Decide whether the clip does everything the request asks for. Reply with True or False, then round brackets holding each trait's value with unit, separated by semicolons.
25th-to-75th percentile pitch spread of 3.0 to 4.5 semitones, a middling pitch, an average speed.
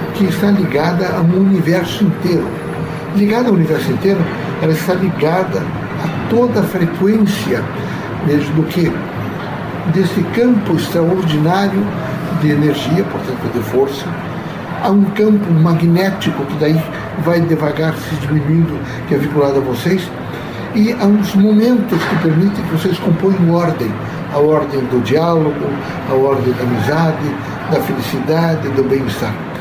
True (4.1 semitones; 165 Hz; 130 wpm)